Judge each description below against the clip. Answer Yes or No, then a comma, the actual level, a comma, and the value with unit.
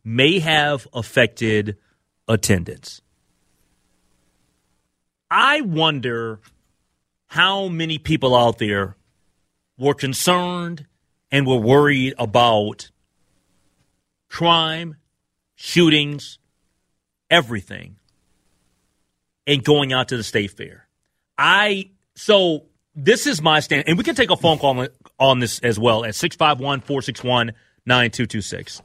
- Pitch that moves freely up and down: Yes, wide, 7.1 semitones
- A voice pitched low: Yes, low, 125 Hz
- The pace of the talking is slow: Yes, slow, 95 wpm